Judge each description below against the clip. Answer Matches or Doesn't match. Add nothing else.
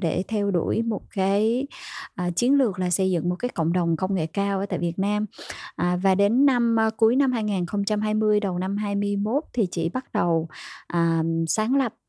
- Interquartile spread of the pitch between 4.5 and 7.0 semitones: Doesn't match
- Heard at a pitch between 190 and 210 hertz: Matches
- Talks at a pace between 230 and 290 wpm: Doesn't match